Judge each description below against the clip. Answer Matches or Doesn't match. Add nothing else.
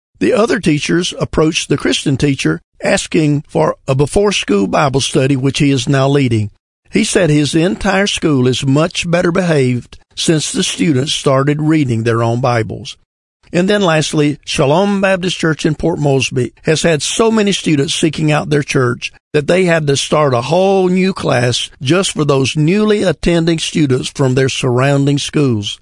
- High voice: Doesn't match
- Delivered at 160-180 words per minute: Matches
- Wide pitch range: Doesn't match